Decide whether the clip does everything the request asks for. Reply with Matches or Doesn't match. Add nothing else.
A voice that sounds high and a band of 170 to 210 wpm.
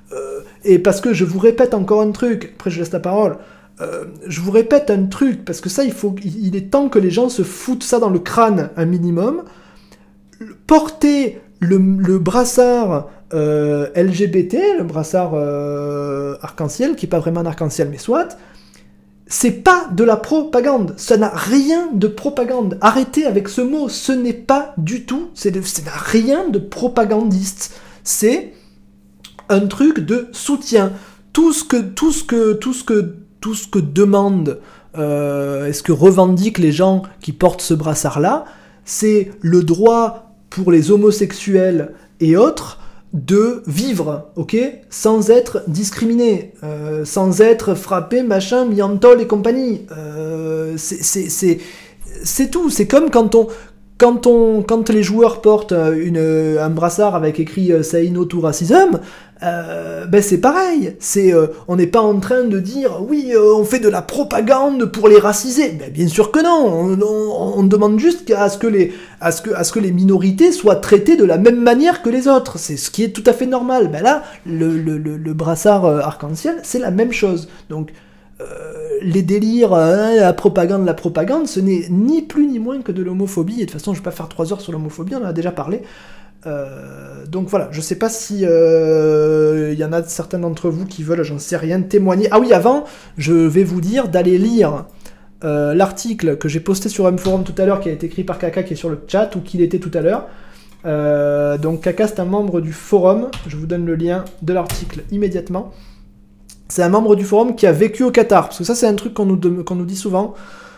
Matches